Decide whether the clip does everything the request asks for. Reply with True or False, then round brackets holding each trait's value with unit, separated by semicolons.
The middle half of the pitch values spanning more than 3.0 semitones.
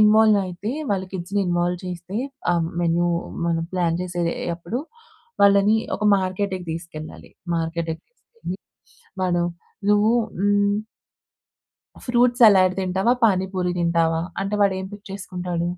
False (2.7 semitones)